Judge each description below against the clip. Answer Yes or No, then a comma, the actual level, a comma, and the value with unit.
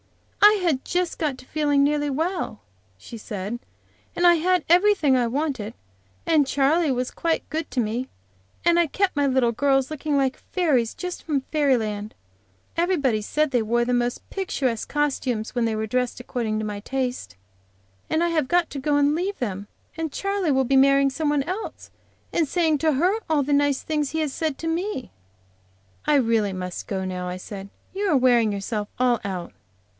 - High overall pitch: Yes, very high, 275 Hz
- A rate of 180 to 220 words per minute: Yes, average, 190 wpm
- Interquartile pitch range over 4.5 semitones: Yes, average, 5.1 semitones